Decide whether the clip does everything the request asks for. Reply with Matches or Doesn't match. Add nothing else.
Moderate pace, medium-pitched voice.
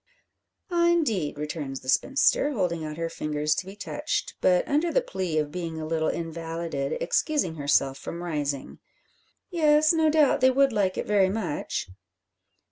Matches